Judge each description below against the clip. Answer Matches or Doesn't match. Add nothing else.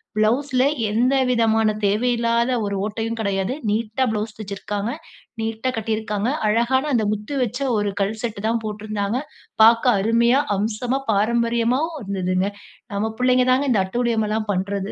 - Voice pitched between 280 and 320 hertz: Doesn't match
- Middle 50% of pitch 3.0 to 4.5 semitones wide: Doesn't match